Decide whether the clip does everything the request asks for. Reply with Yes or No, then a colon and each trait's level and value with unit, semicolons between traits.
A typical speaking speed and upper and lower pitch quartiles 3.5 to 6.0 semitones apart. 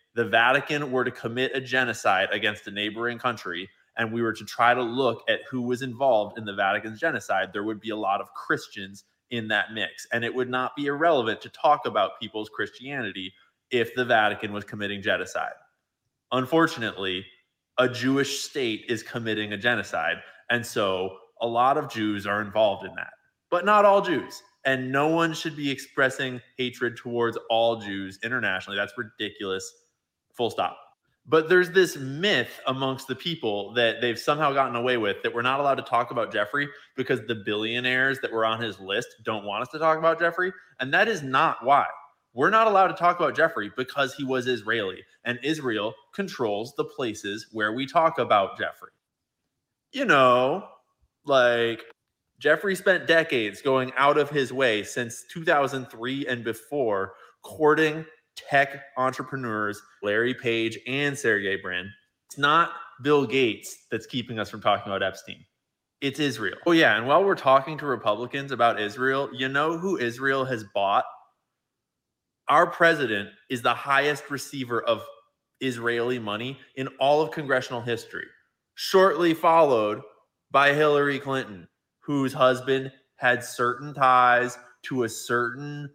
Yes: average, 160 wpm; average, 4.2 semitones